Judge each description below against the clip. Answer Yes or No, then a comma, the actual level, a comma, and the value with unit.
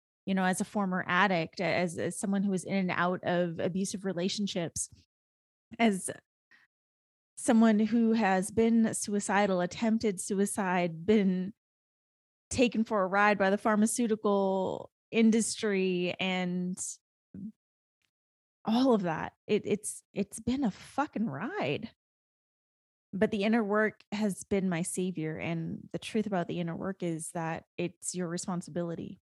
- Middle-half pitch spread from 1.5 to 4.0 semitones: Yes, average, 3.4 semitones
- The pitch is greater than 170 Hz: Yes, high, 190 Hz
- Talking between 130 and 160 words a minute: Yes, slow, 135 wpm